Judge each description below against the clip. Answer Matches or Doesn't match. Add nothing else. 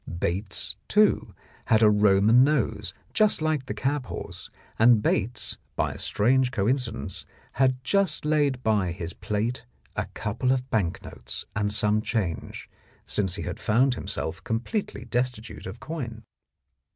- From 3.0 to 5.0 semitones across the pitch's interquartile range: Matches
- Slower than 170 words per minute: Matches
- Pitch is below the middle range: Matches